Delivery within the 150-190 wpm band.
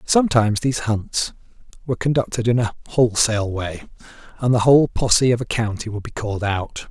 Yes: average, 175 wpm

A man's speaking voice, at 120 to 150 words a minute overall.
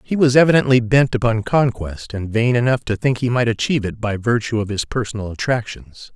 No: male; fast, 205 wpm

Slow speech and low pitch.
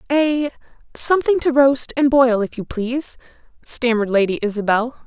No: slow, 130 wpm; very high, 255 Hz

